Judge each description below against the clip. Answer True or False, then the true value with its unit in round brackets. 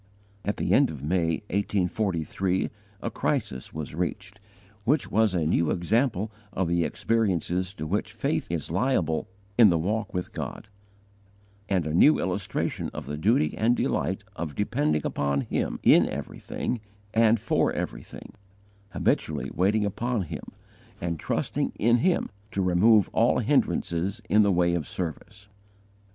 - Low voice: True (95 Hz)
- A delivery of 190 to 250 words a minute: False (145 wpm)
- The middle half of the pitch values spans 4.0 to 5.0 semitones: True (4.4 semitones)